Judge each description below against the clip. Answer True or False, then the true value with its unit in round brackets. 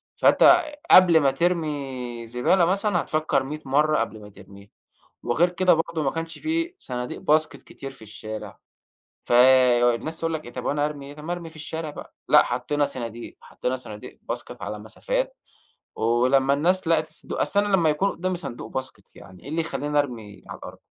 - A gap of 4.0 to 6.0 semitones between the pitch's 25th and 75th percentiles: True (5.2 semitones)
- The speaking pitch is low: False (145 Hz)